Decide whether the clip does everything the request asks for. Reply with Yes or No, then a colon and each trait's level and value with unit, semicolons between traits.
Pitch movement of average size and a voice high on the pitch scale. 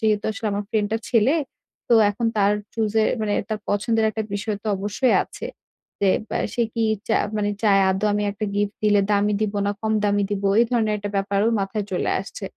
No: narrow, 1.4 semitones; high, 210 Hz